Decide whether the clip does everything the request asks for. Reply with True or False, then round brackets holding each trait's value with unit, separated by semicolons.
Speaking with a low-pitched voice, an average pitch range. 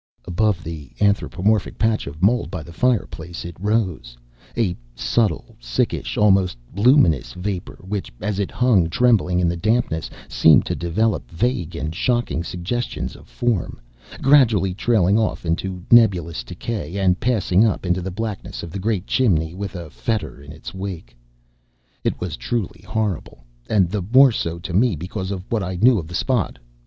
True (95 Hz; 4.5 semitones)